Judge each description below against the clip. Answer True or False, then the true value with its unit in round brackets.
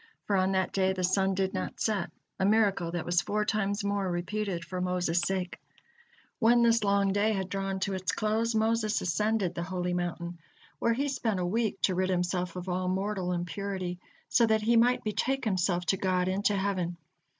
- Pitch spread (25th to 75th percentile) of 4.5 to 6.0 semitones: False (2.8 semitones)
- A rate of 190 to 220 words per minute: True (195 wpm)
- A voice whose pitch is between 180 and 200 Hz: True (190 Hz)